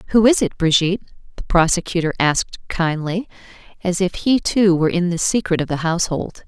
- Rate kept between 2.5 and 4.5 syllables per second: No, 5.8 syllables/s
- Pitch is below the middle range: No, medium, 180 Hz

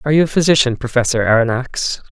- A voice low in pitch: Yes, low, 130 Hz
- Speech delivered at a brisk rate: No, average, 170 wpm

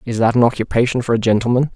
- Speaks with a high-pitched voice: No, low, 120 Hz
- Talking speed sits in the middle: No, fast, 240 wpm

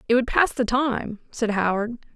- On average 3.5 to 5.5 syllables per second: Yes, 4.6 syllables/s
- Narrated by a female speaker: Yes, female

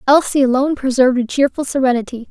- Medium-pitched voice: No, very high, 260 Hz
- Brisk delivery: No, average, 155 wpm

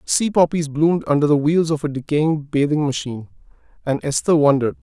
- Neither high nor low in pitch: Yes, medium, 150 Hz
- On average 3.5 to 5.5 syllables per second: No, 5.8 syllables/s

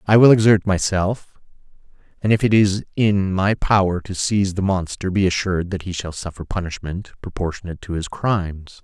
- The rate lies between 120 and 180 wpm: Yes, average, 175 wpm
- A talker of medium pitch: No, very low, 95 Hz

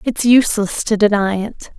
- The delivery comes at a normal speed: Yes, average, 170 wpm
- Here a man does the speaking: No, female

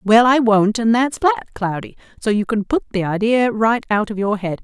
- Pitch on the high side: Yes, high, 220 Hz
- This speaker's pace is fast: Yes, fast, 235 wpm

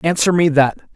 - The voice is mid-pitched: Yes, medium, 155 Hz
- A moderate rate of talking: Yes, average, 190 wpm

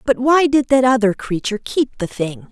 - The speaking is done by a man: No, female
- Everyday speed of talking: No, fast, 215 wpm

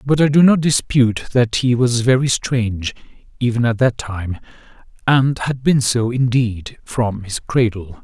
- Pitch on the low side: Yes, low, 120 Hz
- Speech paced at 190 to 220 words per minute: No, average, 165 wpm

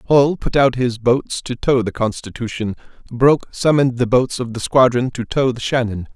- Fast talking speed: No, average, 195 wpm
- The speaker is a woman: No, male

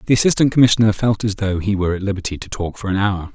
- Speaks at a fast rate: Yes, fast, 270 wpm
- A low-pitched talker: Yes, low, 105 Hz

